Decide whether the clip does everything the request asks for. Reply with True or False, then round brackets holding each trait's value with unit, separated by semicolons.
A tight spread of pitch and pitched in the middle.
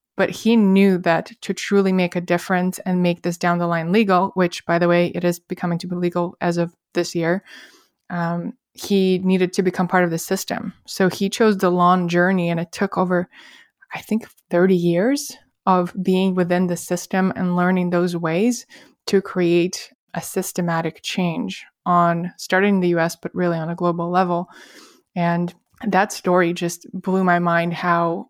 True (1.6 semitones; 180 Hz)